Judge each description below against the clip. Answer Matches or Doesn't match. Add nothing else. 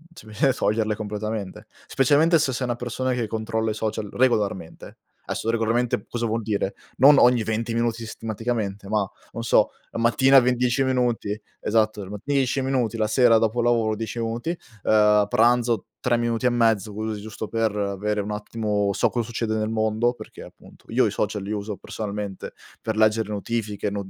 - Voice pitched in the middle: Doesn't match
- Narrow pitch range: Matches